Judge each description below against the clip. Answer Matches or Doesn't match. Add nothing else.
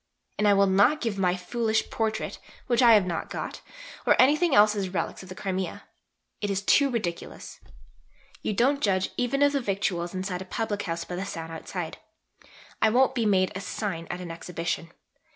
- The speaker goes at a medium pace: Matches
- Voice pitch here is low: Doesn't match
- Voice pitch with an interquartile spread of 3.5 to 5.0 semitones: Matches